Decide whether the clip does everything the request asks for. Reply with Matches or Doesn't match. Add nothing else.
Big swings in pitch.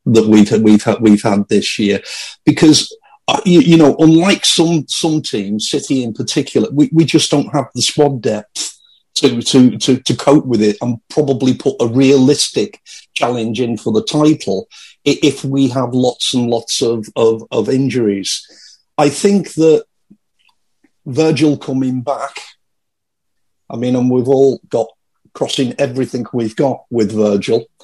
Doesn't match